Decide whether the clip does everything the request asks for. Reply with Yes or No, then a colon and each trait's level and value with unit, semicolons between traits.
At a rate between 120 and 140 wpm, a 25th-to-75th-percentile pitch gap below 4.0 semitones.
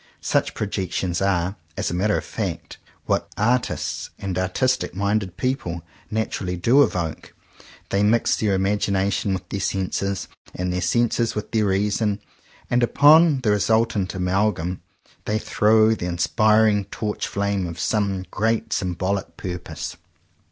Yes: slow, 135 wpm; average, 3.0 semitones